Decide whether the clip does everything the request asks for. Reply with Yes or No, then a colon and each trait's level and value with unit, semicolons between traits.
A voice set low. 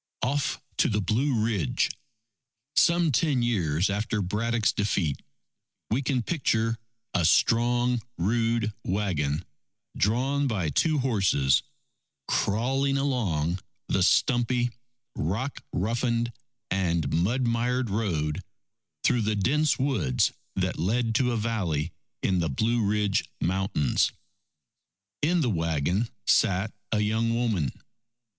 Yes: low, 110 Hz